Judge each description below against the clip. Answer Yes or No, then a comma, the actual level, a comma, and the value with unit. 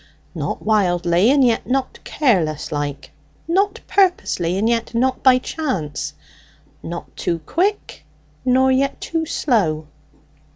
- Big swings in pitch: Yes, wide, 8.0 semitones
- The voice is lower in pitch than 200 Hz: No, high, 240 Hz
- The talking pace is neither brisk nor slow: No, slow, 120 wpm